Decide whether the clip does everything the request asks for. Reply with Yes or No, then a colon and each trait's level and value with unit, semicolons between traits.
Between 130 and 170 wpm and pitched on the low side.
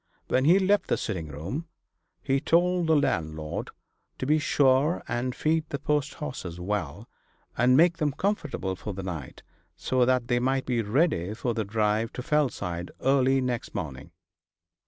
Yes: average, 160 wpm; low, 125 Hz